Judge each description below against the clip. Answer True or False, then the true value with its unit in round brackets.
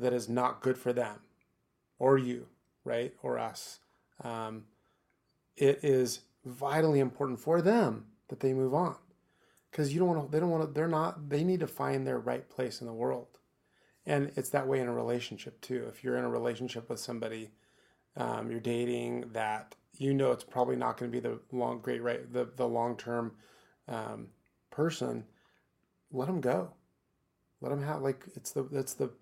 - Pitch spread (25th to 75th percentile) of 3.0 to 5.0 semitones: True (3.3 semitones)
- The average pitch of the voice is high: False (125 Hz)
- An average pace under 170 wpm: False (185 wpm)